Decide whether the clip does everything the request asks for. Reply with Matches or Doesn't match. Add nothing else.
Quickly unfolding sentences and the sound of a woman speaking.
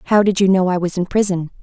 Matches